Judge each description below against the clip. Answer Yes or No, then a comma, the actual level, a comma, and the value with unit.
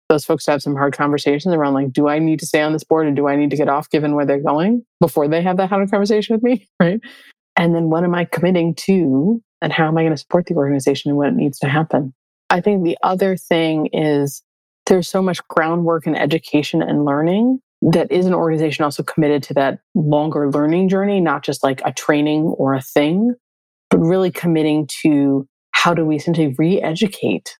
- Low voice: No, medium, 160 Hz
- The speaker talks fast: Yes, fast, 220 wpm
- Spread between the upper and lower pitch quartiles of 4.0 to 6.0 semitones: No, average, 3.3 semitones